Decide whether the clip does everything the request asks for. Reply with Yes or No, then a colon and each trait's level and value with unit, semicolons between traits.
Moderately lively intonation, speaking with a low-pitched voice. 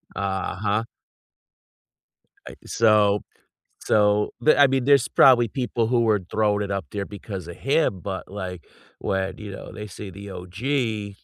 Yes: average, 3.0 semitones; low, 105 Hz